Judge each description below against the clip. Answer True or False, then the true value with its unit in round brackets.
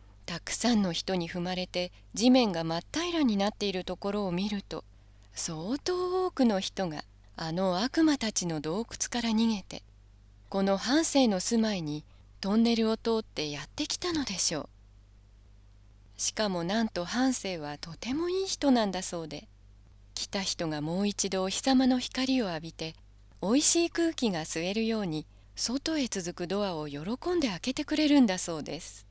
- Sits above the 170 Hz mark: True (190 Hz)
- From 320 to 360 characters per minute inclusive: False (310 characters per minute)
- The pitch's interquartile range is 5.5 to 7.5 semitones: False (8.1 semitones)